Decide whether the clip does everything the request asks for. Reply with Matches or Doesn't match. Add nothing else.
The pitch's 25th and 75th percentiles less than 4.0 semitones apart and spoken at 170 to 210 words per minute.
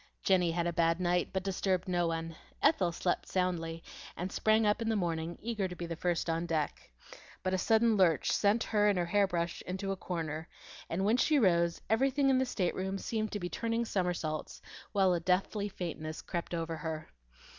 Matches